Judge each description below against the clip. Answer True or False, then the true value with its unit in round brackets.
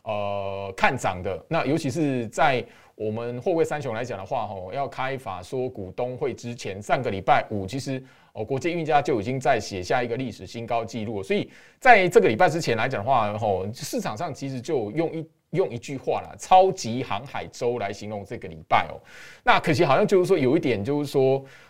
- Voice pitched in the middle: False (130 Hz)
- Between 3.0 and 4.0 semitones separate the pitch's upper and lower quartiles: False (5.5 semitones)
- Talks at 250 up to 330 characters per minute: True (305 characters per minute)